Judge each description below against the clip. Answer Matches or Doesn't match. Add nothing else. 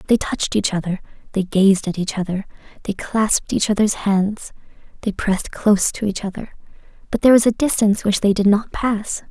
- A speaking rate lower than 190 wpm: Doesn't match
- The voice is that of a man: Doesn't match